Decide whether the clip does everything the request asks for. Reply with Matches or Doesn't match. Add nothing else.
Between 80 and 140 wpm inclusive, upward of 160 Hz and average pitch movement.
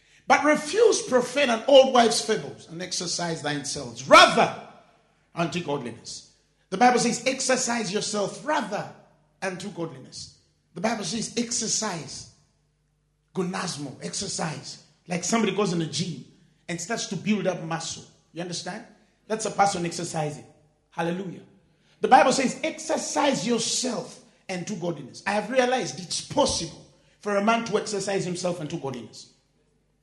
Doesn't match